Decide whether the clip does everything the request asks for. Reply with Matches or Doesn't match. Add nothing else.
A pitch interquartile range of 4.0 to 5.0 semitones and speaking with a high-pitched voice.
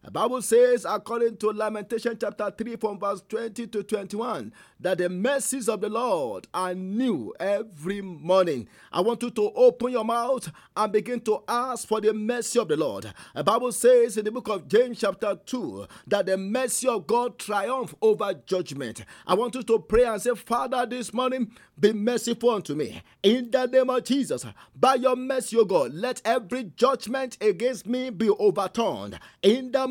Doesn't match